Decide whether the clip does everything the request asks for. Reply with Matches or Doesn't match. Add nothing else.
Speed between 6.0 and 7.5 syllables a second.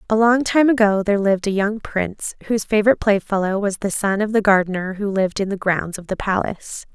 Matches